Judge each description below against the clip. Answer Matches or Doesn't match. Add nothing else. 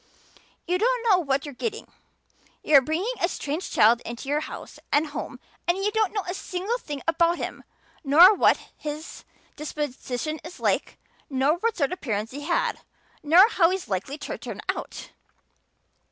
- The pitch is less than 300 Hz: Doesn't match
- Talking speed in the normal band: Matches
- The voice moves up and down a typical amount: Matches